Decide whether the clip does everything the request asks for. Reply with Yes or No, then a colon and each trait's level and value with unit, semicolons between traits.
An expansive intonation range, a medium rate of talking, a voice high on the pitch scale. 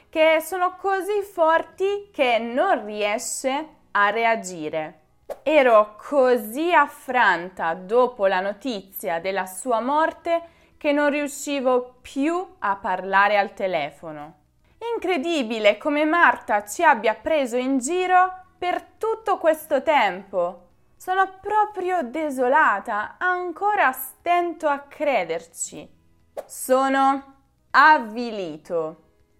No: wide, 8.7 semitones; slow, 95 wpm; very high, 275 Hz